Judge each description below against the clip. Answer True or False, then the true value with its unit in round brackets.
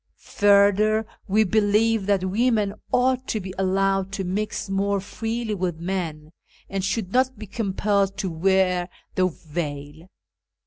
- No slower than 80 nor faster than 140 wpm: True (135 wpm)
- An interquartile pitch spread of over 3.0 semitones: False (2.5 semitones)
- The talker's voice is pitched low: False (195 Hz)